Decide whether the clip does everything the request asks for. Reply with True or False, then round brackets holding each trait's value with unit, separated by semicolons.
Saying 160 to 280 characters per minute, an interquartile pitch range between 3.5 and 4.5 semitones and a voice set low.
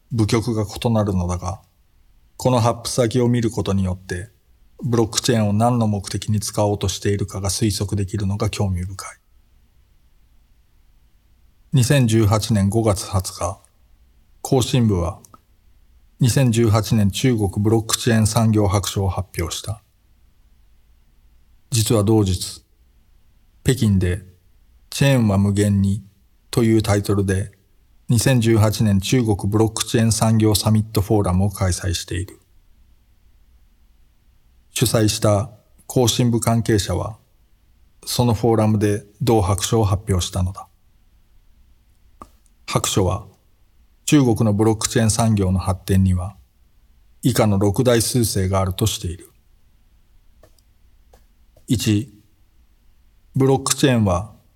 True (230 characters per minute; 3.9 semitones; 100 Hz)